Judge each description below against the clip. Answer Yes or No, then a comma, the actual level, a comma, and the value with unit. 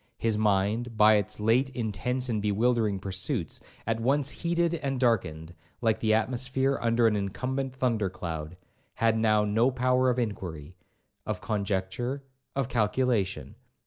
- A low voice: Yes, low, 115 Hz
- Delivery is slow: No, average, 145 wpm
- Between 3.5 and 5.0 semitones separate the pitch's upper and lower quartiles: Yes, average, 4.0 semitones